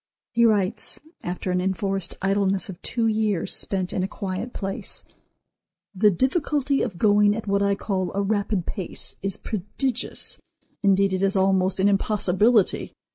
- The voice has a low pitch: No, high, 195 Hz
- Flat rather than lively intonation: Yes, narrow, 2.1 semitones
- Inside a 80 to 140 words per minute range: No, average, 150 wpm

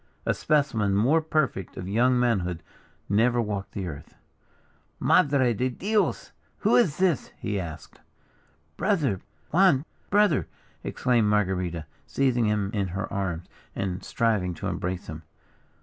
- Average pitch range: No, wide, 6.5 semitones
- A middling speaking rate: No, slow, 130 wpm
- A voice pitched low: Yes, low, 105 Hz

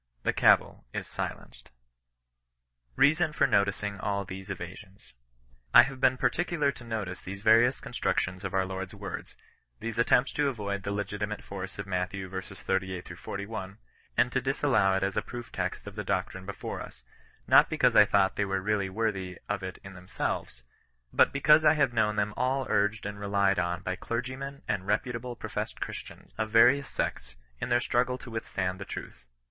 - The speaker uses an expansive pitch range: No, average, 3.7 semitones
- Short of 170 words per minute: No, average, 175 wpm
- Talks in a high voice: No, low, 100 Hz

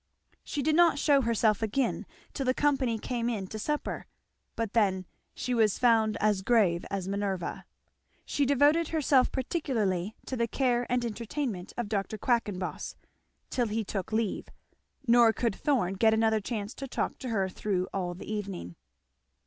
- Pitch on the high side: Yes, high, 225 Hz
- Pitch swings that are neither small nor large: Yes, average, 4.1 semitones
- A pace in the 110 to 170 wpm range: Yes, average, 160 wpm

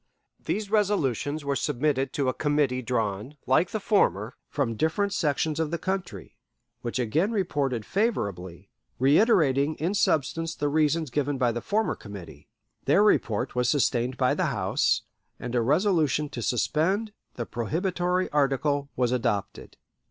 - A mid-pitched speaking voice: Yes, medium, 145 Hz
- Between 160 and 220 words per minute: No, average, 145 wpm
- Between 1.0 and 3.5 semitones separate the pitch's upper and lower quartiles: No, average, 5.3 semitones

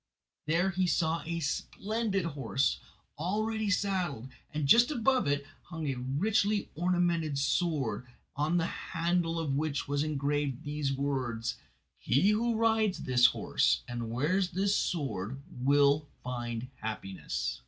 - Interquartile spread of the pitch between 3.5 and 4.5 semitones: No, average, 5.3 semitones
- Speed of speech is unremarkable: No, slow, 130 wpm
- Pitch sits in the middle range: Yes, medium, 155 Hz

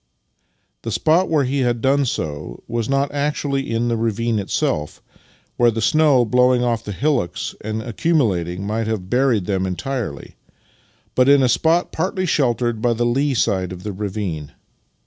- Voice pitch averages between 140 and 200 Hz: No, low, 120 Hz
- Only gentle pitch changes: No, average, 4.9 semitones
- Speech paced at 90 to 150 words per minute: No, average, 170 wpm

